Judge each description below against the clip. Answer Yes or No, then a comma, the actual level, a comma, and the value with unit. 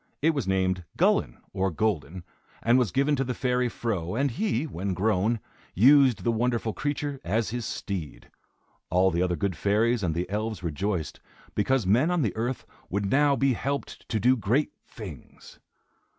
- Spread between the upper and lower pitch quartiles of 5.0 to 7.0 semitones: Yes, wide, 5.5 semitones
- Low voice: Yes, low, 110 Hz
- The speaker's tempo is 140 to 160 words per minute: No, average, 170 wpm